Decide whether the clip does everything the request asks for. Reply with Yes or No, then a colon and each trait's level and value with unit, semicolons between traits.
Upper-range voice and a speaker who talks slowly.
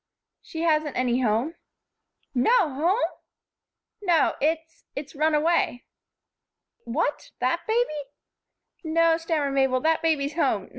Yes: very high, 305 Hz; slow, 110 wpm